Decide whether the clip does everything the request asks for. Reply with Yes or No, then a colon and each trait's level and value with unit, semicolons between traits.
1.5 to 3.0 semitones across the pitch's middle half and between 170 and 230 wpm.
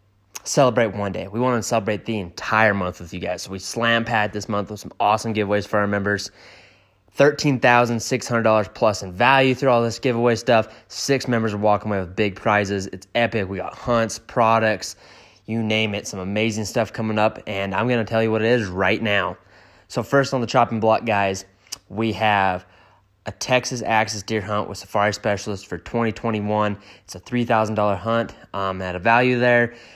Yes: average, 2.7 semitones; average, 200 wpm